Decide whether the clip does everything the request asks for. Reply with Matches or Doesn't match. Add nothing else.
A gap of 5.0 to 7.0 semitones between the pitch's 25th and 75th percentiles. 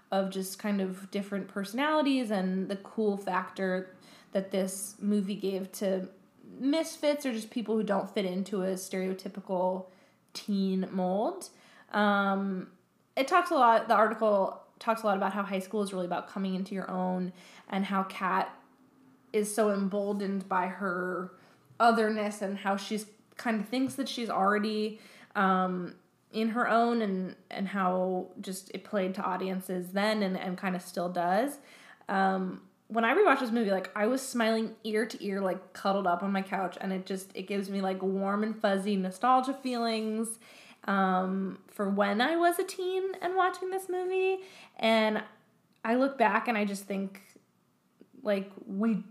Doesn't match